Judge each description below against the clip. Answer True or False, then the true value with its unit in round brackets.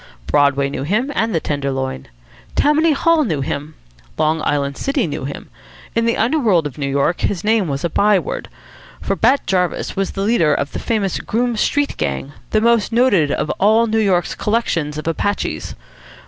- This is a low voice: False (190 Hz)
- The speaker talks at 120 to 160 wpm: False (180 wpm)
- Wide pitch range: True (7.9 semitones)